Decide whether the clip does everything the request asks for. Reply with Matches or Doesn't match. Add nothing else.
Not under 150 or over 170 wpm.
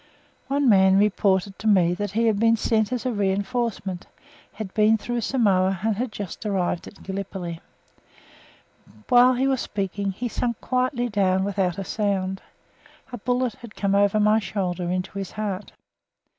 Matches